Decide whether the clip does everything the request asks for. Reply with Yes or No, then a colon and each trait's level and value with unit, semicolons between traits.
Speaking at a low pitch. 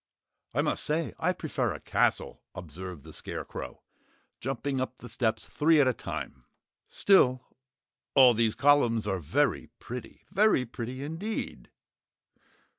Yes: low, 130 Hz